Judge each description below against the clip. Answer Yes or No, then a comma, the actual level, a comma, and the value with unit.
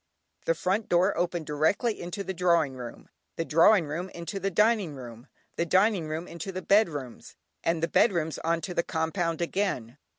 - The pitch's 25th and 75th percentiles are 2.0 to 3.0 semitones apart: No, average, 3.4 semitones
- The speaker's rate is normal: Yes, average, 175 wpm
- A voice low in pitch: No, medium, 170 Hz